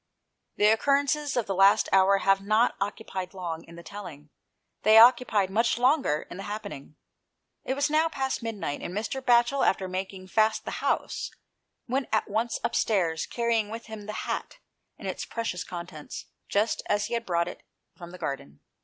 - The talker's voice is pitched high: Yes, high, 210 Hz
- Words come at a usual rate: Yes, average, 175 wpm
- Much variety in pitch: No, average, 4.2 semitones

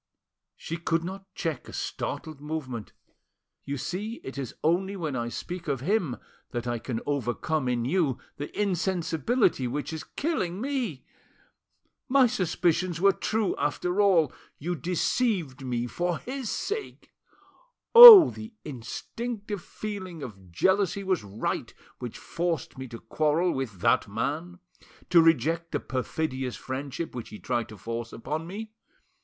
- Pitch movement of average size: No, wide, 6.7 semitones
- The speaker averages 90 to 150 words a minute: Yes, average, 140 wpm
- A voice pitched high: No, medium, 165 Hz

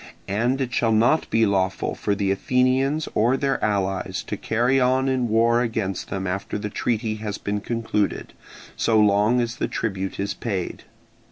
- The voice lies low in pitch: Yes, low, 110 Hz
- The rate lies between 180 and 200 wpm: No, average, 165 wpm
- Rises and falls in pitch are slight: No, average, 3.7 semitones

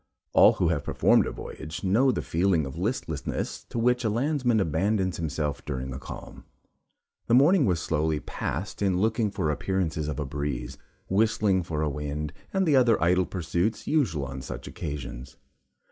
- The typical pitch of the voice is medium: No, very low, 85 Hz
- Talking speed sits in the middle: Yes, average, 170 wpm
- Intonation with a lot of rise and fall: Yes, wide, 6.7 semitones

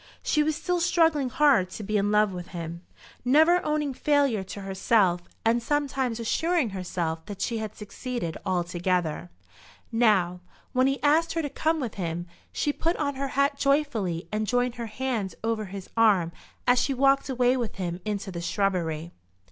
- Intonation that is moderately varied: No, wide, 6.8 semitones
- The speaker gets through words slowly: No, average, 170 wpm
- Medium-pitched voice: No, high, 225 Hz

